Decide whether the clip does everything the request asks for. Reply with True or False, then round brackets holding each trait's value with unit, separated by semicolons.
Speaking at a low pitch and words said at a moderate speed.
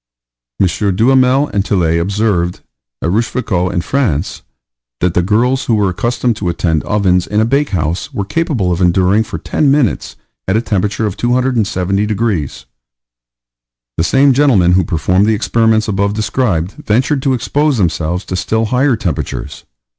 True (105 Hz; 150 wpm)